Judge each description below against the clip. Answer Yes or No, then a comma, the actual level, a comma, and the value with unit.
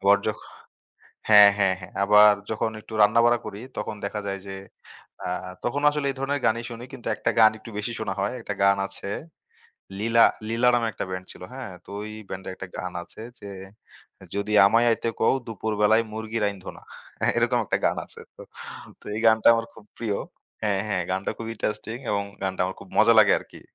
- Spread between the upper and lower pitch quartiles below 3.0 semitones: Yes, narrow, 2.4 semitones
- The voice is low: Yes, low, 105 Hz